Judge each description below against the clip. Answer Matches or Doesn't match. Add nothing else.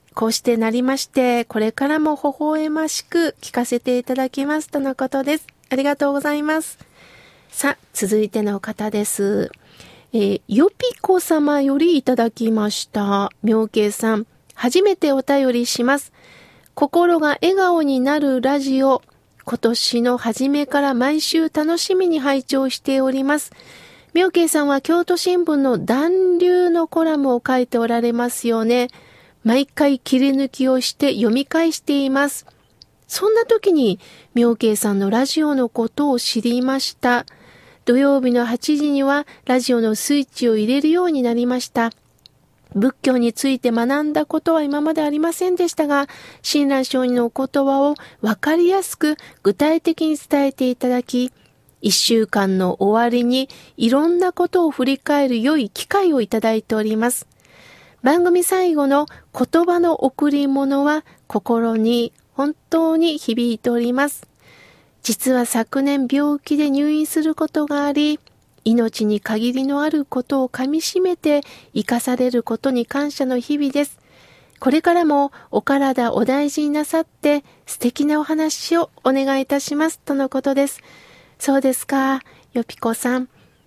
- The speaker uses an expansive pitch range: Doesn't match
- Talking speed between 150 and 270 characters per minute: Doesn't match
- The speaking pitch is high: Matches